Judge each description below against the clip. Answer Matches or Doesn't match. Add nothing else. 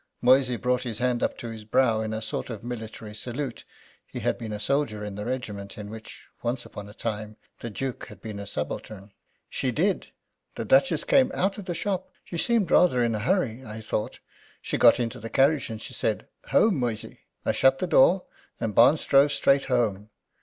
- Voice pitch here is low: Matches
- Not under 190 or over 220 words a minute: Matches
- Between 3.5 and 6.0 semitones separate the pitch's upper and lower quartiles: Matches